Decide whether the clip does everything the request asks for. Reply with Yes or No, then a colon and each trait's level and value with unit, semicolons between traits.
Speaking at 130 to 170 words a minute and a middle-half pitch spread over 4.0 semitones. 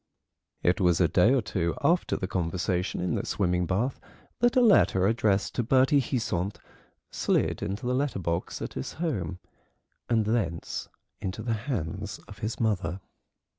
Yes: average, 160 wpm; wide, 5.4 semitones